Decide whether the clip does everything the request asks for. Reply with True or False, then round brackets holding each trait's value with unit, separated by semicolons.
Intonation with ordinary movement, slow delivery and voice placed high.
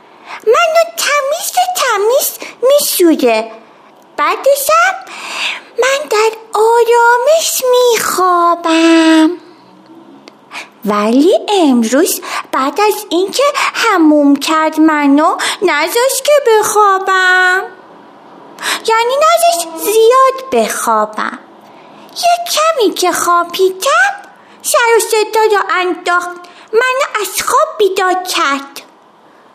True (5.0 semitones; 85 wpm; 360 Hz)